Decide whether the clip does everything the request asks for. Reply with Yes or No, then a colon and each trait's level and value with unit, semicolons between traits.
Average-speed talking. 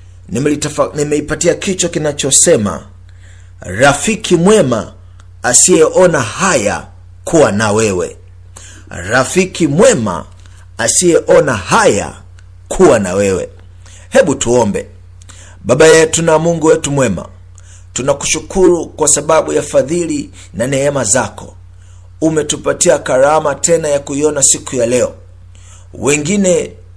No: slow, 95 wpm